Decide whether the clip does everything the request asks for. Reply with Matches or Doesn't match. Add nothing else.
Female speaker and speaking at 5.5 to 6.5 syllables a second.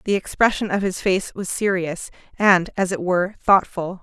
Doesn't match